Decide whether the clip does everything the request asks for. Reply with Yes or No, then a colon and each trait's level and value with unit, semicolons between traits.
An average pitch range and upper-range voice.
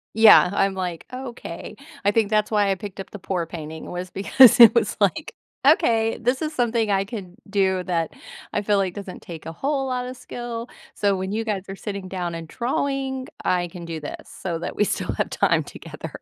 Yes: average, 4.4 semitones; high, 200 Hz